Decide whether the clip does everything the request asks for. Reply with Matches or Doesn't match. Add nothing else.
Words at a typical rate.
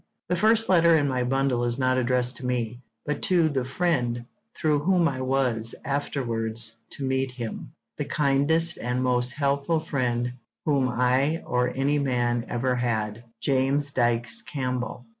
Matches